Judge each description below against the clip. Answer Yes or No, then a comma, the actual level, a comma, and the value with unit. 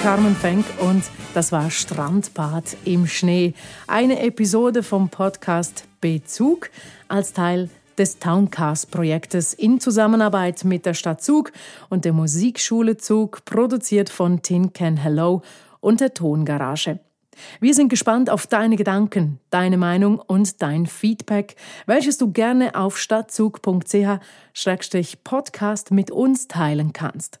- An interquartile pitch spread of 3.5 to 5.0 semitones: Yes, average, 4.2 semitones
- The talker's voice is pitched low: No, high, 195 Hz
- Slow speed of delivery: Yes, slow, 120 wpm